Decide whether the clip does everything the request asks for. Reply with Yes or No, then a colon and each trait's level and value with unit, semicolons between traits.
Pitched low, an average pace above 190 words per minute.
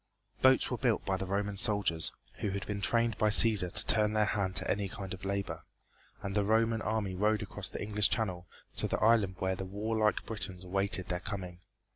Yes: low, 100 Hz; fast, 205 wpm